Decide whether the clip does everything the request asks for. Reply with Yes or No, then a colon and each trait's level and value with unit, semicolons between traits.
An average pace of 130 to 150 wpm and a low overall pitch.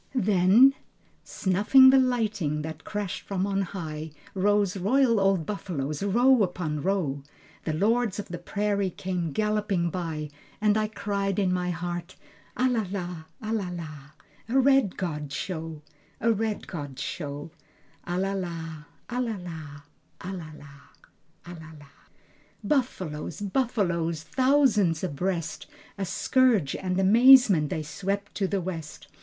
No: average, 140 wpm; medium, 185 Hz